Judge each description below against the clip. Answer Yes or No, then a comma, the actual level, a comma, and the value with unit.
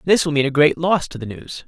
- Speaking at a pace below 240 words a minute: No, fast, 325 wpm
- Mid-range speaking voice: Yes, medium, 155 Hz